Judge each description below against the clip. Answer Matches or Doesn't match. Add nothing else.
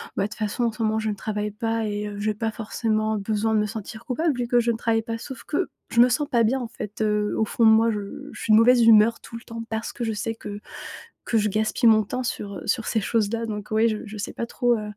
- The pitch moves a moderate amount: Doesn't match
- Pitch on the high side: Matches